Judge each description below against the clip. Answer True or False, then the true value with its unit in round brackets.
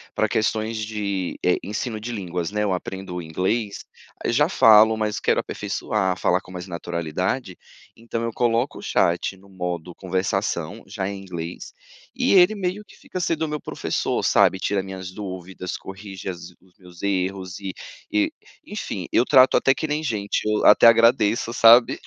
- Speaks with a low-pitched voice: True (100 Hz)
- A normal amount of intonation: True (3.9 semitones)